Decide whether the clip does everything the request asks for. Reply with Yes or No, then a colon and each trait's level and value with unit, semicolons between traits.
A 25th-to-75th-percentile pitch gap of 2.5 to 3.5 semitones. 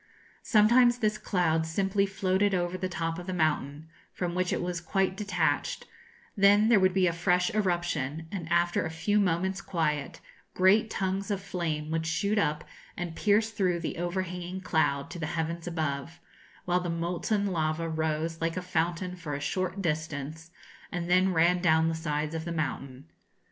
Yes: average, 2.8 semitones